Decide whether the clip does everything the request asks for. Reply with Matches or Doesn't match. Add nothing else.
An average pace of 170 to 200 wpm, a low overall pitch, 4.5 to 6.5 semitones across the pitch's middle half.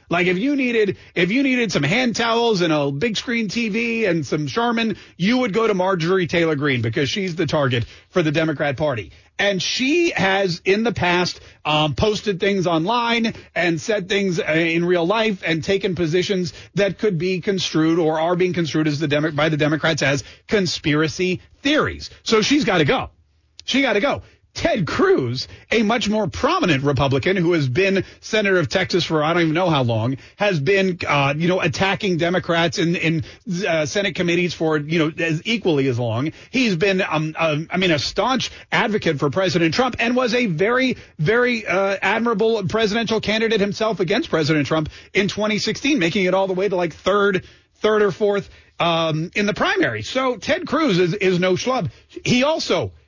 Doesn't match